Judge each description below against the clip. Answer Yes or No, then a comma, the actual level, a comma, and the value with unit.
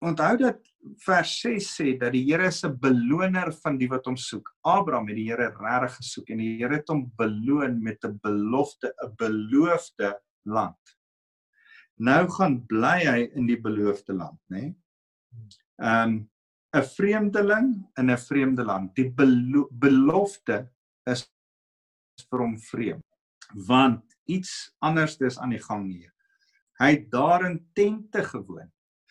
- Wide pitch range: Yes, wide, 6.9 semitones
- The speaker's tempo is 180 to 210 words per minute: No, average, 140 wpm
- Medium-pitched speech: No, low, 130 Hz